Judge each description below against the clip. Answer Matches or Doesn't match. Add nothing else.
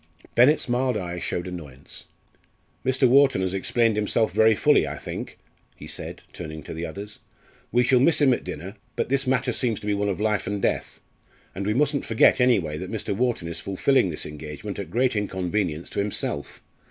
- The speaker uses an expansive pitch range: Matches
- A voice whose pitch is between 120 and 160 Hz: Doesn't match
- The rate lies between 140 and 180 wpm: Doesn't match